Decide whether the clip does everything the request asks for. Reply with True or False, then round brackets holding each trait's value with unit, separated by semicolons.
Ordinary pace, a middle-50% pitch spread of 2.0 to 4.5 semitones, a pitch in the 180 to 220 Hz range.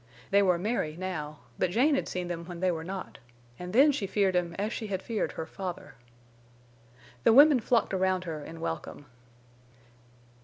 True (180 wpm; 3.7 semitones; 185 Hz)